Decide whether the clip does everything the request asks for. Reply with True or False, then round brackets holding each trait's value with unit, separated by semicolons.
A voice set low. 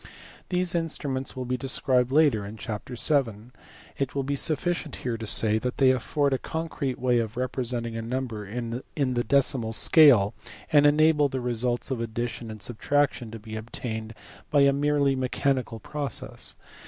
True (125 Hz)